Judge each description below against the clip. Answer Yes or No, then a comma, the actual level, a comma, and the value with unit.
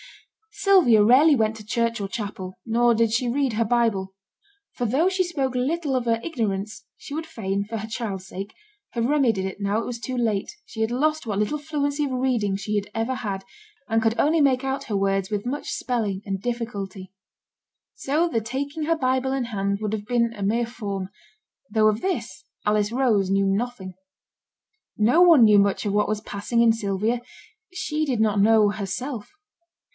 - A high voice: Yes, high, 225 Hz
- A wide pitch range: No, average, 4.2 semitones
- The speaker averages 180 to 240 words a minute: Yes, average, 190 wpm